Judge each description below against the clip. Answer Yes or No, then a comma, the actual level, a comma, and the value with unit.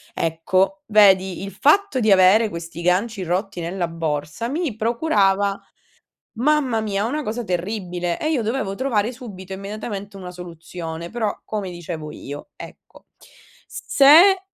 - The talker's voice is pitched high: Yes, high, 200 Hz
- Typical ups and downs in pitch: Yes, average, 4.7 semitones